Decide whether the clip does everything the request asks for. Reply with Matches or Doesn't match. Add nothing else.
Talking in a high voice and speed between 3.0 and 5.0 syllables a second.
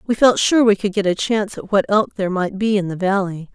Doesn't match